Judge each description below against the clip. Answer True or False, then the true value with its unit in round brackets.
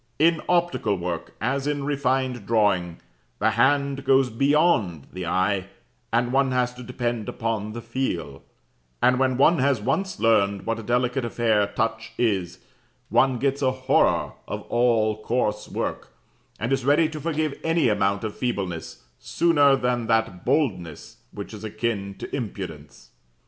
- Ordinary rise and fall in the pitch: True (4.3 semitones)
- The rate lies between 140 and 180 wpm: True (150 wpm)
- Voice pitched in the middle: False (120 Hz)